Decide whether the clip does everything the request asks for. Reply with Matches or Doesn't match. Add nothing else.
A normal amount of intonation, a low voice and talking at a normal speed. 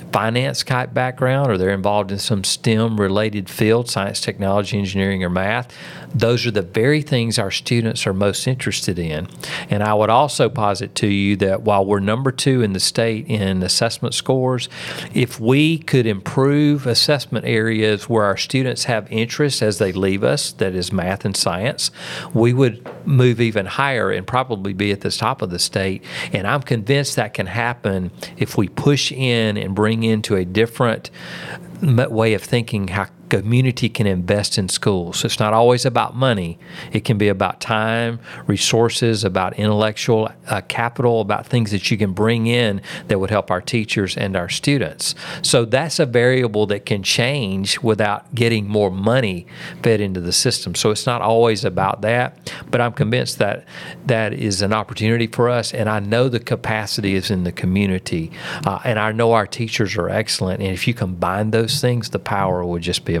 Matches